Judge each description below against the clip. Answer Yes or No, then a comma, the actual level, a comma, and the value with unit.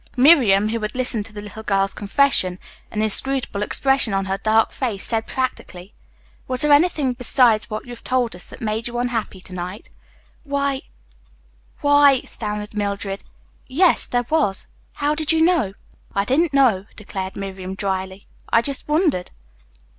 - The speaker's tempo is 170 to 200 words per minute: No, average, 160 wpm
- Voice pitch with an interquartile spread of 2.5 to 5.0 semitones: No, wide, 5.5 semitones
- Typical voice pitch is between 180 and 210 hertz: No, high, 225 Hz